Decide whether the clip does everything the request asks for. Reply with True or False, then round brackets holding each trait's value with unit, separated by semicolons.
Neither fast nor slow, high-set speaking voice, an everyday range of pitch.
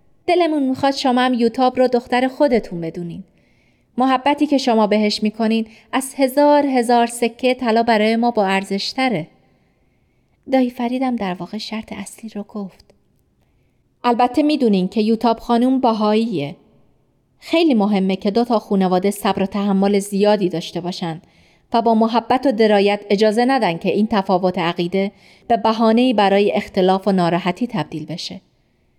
True (140 wpm; 220 Hz; 4.1 semitones)